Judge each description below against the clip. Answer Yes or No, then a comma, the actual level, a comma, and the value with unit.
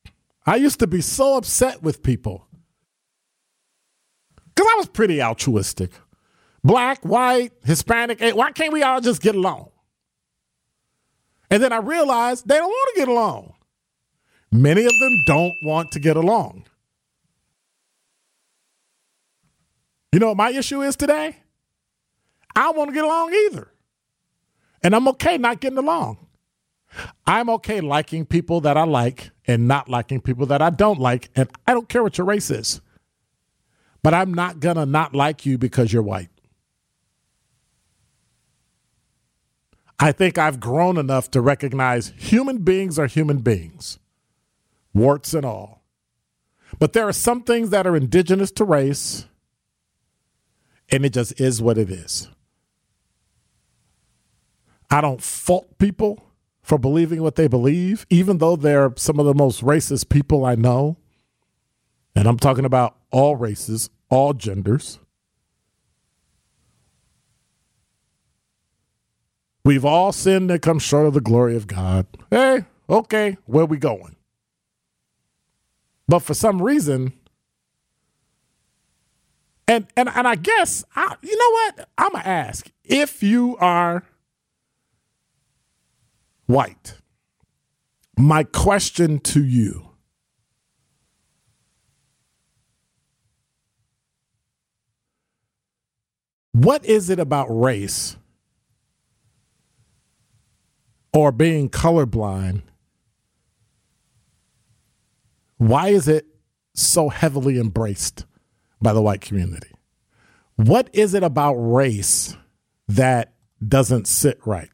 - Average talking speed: No, slow, 115 wpm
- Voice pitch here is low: No, medium, 150 Hz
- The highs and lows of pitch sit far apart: Yes, wide, 8.8 semitones